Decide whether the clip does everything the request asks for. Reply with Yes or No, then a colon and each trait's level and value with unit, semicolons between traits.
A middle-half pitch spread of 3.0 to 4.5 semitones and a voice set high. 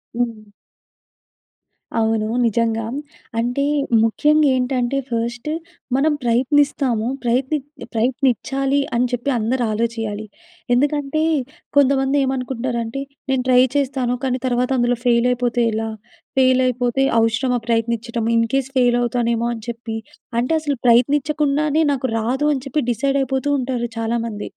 No: narrow, 2.6 semitones; high, 245 Hz